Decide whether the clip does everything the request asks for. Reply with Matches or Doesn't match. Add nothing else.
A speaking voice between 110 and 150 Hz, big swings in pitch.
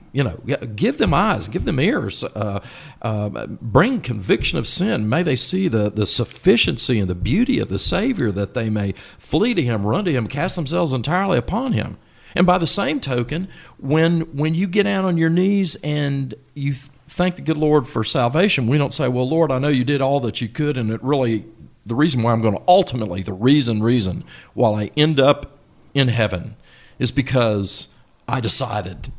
Matches